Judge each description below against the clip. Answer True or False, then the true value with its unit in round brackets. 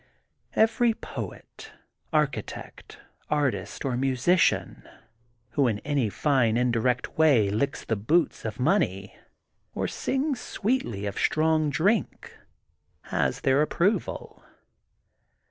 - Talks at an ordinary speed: False (105 wpm)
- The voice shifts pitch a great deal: True (6.4 semitones)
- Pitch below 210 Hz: True (140 Hz)